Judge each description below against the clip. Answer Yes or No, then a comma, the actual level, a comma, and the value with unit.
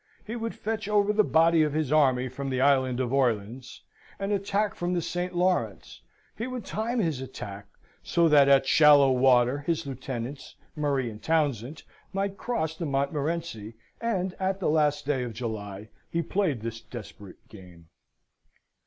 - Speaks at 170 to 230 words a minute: No, average, 160 wpm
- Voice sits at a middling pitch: Yes, medium, 145 Hz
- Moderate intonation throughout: No, wide, 6.0 semitones